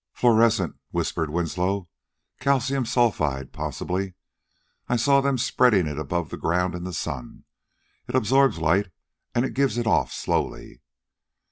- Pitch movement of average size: No, wide, 6.3 semitones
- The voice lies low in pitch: Yes, low, 100 Hz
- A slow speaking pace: Yes, slow, 125 wpm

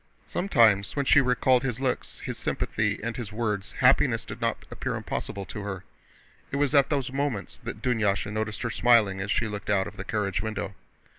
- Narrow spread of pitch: No, average, 3.9 semitones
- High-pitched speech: No, low, 110 Hz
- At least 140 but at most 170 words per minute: No, average, 195 wpm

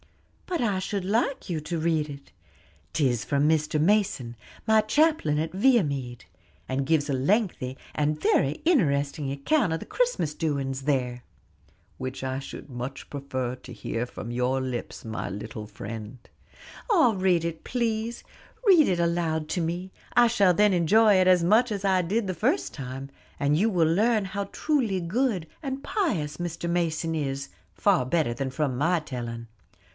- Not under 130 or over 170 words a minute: Yes, average, 165 wpm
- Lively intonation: Yes, wide, 7.0 semitones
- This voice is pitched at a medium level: Yes, medium, 160 Hz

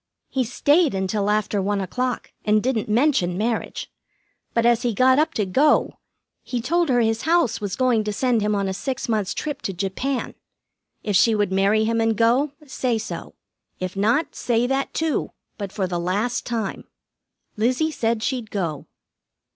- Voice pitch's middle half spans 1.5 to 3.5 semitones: No, average, 4.0 semitones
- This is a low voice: No, high, 225 Hz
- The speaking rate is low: No, average, 175 wpm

